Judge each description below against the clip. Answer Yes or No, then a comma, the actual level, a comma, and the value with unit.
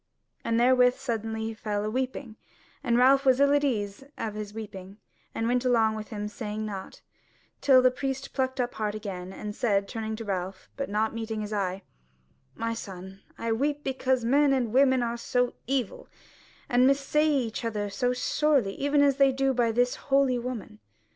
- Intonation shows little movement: No, average, 3.7 semitones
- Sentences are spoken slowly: No, average, 185 wpm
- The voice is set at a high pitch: Yes, high, 235 Hz